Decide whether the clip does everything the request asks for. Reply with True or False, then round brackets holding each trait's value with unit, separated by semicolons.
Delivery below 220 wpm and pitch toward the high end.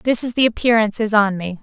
False (260 wpm; 220 Hz)